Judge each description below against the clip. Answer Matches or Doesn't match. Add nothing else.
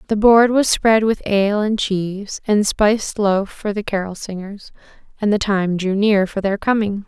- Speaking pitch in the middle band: Doesn't match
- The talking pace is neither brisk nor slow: Matches